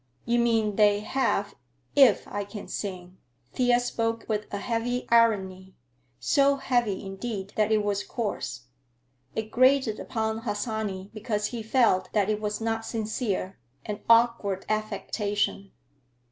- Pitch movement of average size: No, narrow, 2.3 semitones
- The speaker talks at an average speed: No, slow, 130 wpm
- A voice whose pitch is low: No, high, 215 Hz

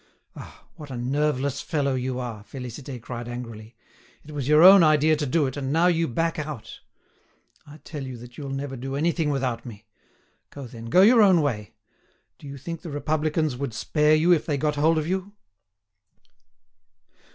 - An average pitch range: Yes, average, 3.8 semitones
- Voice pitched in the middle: Yes, medium, 145 Hz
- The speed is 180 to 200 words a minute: Yes, average, 185 wpm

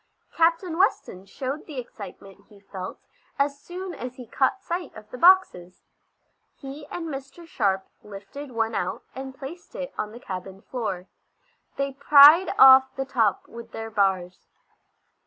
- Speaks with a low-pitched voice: No, very high, 260 Hz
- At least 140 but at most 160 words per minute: Yes, average, 150 wpm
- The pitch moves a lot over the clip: Yes, wide, 6.7 semitones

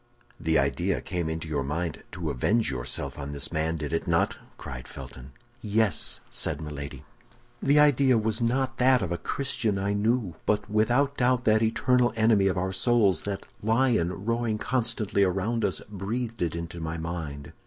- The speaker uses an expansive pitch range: Yes, wide, 6.3 semitones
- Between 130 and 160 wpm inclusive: No, average, 170 wpm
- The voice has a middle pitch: No, low, 100 Hz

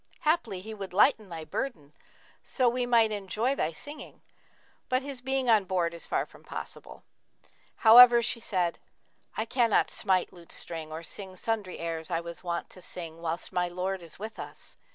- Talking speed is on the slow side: No, average, 175 wpm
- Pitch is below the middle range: No, high, 190 Hz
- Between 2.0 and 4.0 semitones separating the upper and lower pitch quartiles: No, wide, 5.6 semitones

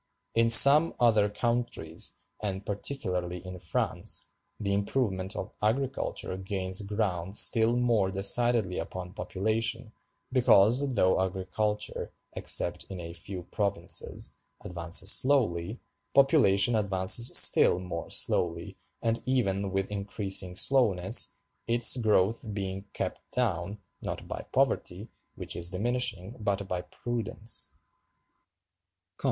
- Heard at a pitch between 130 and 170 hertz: No, low, 100 Hz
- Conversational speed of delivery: No, slow, 110 wpm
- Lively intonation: No, average, 3.8 semitones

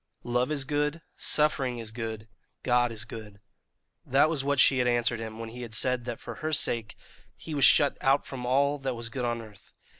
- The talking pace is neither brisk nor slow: No, fast, 210 wpm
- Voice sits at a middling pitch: No, low, 125 Hz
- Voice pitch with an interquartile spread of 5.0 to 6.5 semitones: No, average, 3.4 semitones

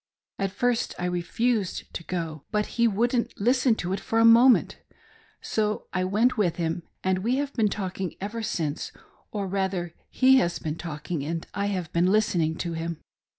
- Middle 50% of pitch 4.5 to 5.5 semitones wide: Yes, average, 4.8 semitones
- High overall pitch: Yes, high, 195 Hz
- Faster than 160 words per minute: Yes, average, 180 wpm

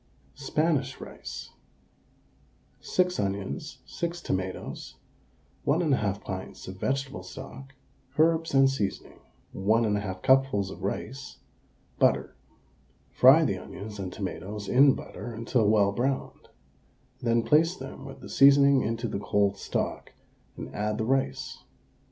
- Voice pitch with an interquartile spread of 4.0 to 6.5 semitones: Yes, average, 5.2 semitones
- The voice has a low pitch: Yes, low, 120 Hz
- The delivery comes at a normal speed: No, slow, 120 wpm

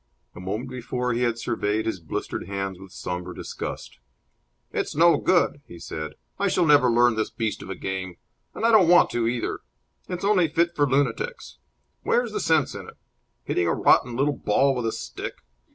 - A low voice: Yes, low, 120 Hz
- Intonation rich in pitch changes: Yes, wide, 8.3 semitones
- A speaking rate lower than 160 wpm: No, average, 190 wpm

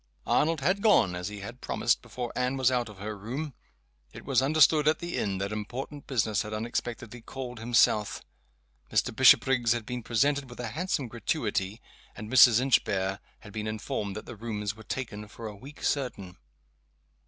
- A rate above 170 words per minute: Yes, average, 180 wpm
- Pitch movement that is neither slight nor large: Yes, average, 3.9 semitones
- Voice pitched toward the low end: Yes, low, 115 Hz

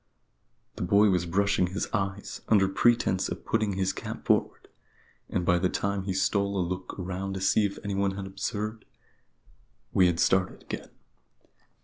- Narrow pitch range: Yes, narrow, 1.5 semitones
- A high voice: No, very low, 95 Hz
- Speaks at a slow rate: No, average, 160 wpm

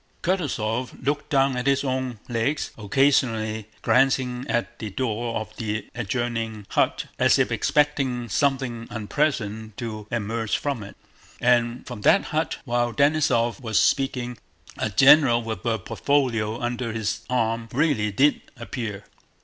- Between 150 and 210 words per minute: No, slow, 135 wpm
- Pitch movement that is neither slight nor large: Yes, average, 3.4 semitones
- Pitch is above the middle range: No, low, 120 Hz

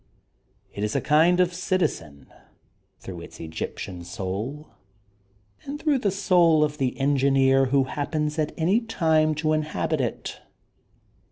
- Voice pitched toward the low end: No, medium, 150 Hz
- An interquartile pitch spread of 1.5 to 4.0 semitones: No, average, 4.5 semitones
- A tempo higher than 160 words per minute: No, average, 140 wpm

